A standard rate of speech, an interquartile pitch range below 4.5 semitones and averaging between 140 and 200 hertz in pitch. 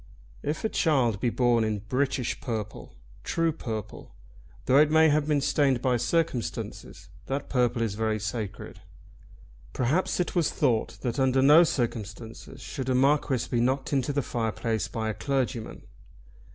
No: average, 150 wpm; average, 4.1 semitones; low, 125 Hz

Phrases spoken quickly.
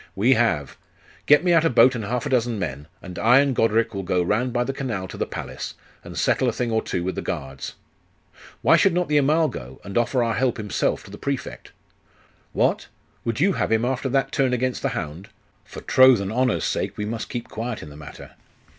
Yes: fast, 225 wpm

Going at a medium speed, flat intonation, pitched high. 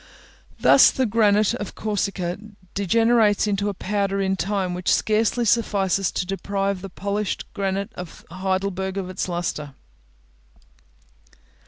No: slow, 130 wpm; narrow, 1.8 semitones; high, 195 Hz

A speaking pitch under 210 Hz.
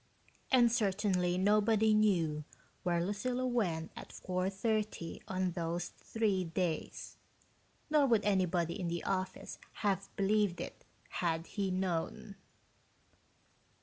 Yes: high, 190 Hz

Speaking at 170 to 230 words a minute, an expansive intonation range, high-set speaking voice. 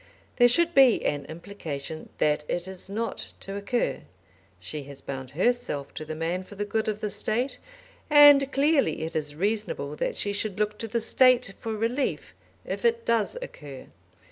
Yes: average, 175 wpm; wide, 7.5 semitones; high, 205 Hz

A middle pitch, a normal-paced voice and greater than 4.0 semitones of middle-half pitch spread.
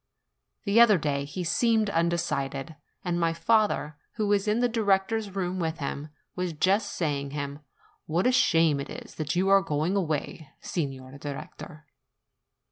Yes: medium, 170 Hz; average, 160 wpm; average, 5.2 semitones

